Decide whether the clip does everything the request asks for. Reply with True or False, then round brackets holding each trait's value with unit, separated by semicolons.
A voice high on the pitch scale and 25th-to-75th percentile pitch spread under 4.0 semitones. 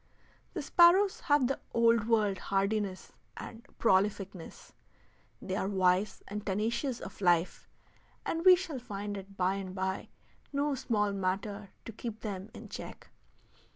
True (205 Hz; 3.4 semitones)